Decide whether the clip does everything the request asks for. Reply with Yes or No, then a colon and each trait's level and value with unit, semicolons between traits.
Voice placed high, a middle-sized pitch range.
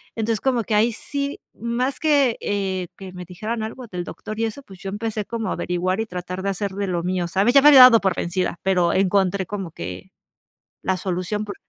Yes: high, 200 Hz; average, 3.7 semitones